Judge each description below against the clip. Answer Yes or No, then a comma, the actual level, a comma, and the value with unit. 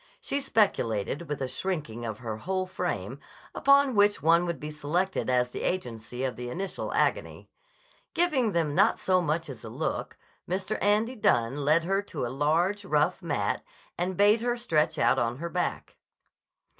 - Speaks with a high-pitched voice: No, medium, 170 Hz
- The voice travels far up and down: Yes, wide, 6.8 semitones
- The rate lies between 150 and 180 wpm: Yes, average, 170 wpm